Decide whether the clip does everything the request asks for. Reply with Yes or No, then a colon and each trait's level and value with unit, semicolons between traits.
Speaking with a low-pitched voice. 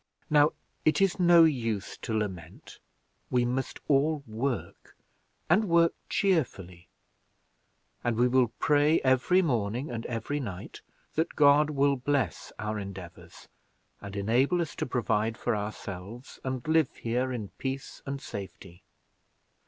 Yes: low, 125 Hz